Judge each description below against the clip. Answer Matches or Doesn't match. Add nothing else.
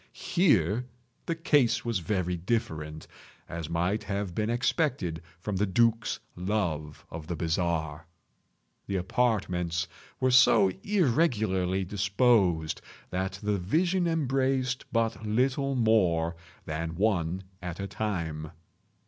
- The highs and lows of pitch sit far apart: Matches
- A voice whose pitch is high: Doesn't match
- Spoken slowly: Matches